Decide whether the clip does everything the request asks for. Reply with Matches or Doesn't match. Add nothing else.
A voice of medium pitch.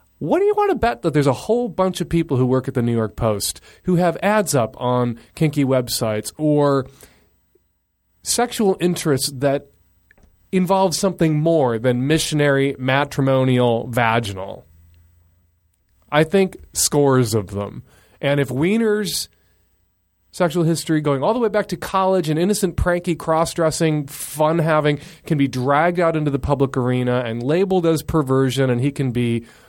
Matches